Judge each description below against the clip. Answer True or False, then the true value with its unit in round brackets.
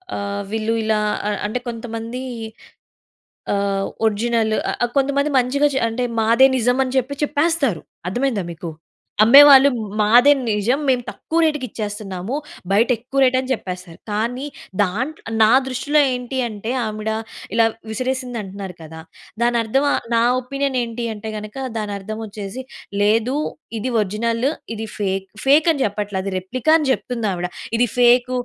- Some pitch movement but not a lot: True (3.9 semitones)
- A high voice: True (230 Hz)